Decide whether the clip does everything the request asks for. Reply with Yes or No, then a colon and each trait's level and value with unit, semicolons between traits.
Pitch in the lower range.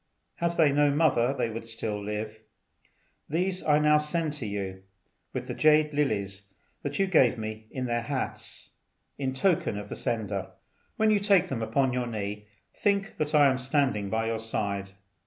Yes: low, 130 Hz